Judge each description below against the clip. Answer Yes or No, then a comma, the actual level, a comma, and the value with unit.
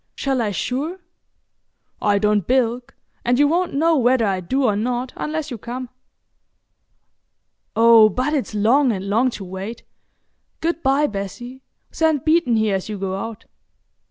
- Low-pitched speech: No, high, 245 Hz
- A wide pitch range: No, average, 4.6 semitones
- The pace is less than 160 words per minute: Yes, average, 150 wpm